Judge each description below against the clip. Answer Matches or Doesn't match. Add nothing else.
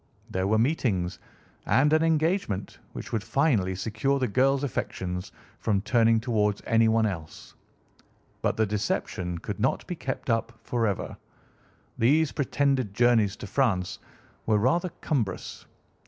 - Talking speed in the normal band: Doesn't match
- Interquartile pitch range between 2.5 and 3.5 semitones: Doesn't match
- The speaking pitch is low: Matches